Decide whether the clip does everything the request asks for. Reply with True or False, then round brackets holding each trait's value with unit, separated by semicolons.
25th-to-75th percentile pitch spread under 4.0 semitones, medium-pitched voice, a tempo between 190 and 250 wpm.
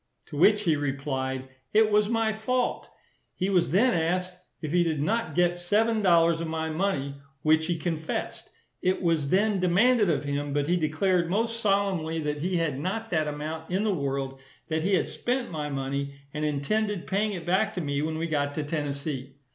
False (5.0 semitones; 165 Hz; 195 wpm)